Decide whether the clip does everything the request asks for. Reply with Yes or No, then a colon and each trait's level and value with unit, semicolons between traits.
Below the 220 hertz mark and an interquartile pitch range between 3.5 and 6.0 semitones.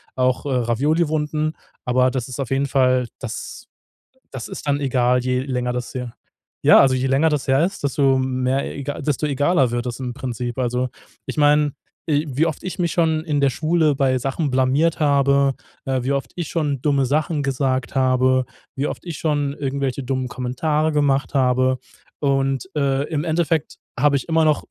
No: low, 135 Hz; narrow, 2.6 semitones